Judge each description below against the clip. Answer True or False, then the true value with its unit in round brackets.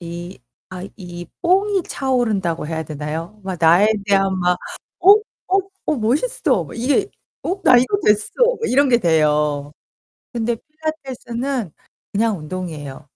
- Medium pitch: False (210 Hz)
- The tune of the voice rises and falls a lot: True (8.0 semitones)